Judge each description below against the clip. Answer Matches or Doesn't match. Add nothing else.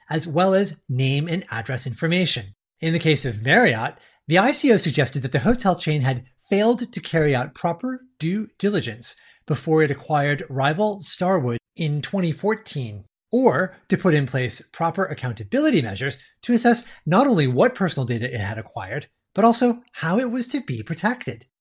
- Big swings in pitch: Matches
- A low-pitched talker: Doesn't match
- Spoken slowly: Doesn't match